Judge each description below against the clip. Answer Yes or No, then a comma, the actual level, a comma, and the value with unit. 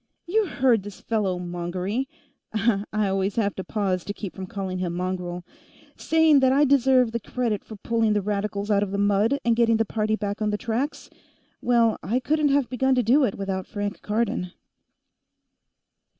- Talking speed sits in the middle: Yes, average, 180 wpm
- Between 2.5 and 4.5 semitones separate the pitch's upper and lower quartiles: Yes, average, 3.9 semitones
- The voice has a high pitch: Yes, high, 215 Hz